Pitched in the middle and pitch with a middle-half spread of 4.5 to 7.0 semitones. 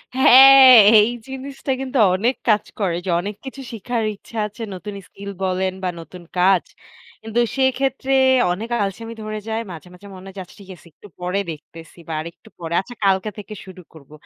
No: high, 200 Hz; average, 4.9 semitones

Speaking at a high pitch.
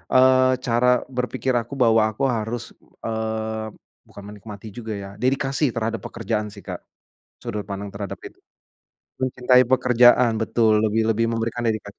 No: low, 115 Hz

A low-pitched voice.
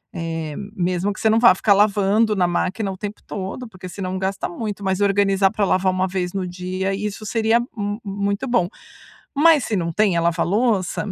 No: high, 195 Hz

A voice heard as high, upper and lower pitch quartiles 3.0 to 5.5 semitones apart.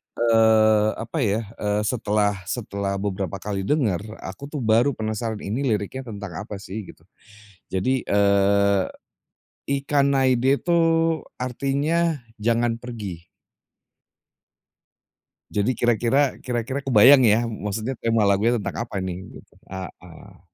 No: low, 110 Hz; average, 4.0 semitones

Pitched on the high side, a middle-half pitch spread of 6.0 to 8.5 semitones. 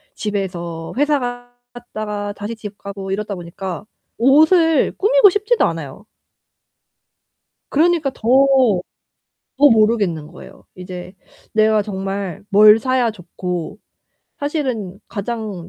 No: high, 210 Hz; average, 5.3 semitones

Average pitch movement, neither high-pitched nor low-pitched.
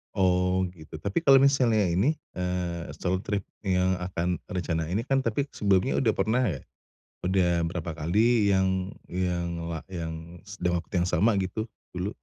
No: average, 3.0 semitones; very low, 95 Hz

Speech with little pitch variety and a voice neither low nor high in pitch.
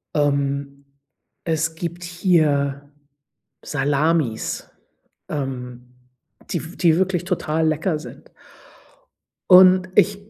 No: average, 3.7 semitones; medium, 155 Hz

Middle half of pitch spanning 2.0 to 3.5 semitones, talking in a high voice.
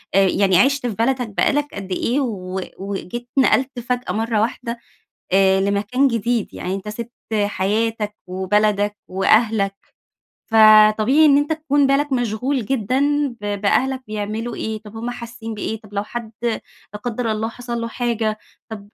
Yes: average, 3.1 semitones; high, 225 Hz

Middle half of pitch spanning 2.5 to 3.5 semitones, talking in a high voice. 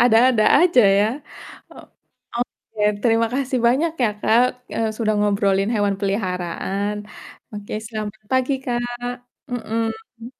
Yes: average, 2.8 semitones; high, 225 Hz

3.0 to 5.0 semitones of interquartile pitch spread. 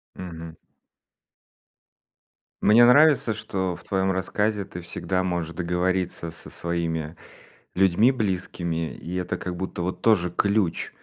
No: narrow, 2.6 semitones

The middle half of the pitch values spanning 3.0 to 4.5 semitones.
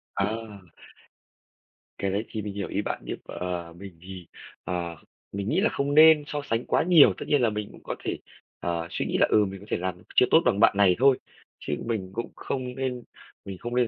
No: average, 5.2 semitones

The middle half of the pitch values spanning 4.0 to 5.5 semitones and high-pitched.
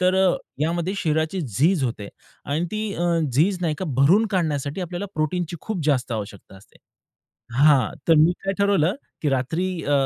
No: average, 4.6 semitones; medium, 160 Hz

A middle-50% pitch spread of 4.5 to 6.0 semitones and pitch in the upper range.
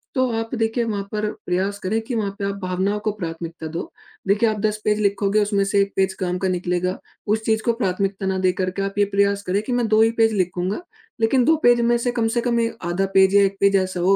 No: average, 2.7 semitones; high, 200 Hz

